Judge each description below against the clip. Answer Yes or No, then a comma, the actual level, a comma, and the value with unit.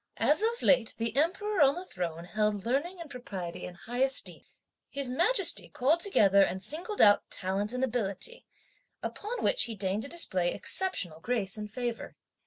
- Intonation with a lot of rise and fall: Yes, wide, 9.0 semitones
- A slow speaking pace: No, average, 170 wpm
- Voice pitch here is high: Yes, high, 245 Hz